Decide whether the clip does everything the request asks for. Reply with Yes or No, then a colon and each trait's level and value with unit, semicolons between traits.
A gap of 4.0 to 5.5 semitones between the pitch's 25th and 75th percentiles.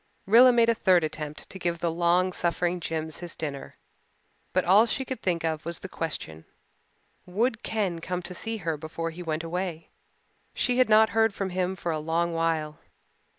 No: average, 3.1 semitones